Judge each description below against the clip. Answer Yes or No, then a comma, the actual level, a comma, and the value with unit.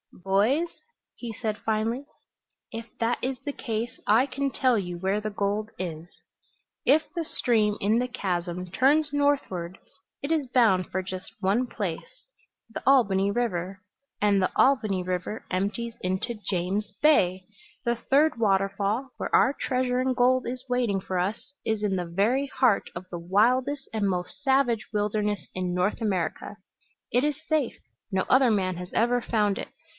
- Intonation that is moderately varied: Yes, average, 4.9 semitones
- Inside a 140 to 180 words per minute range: Yes, average, 160 wpm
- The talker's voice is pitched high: Yes, high, 215 Hz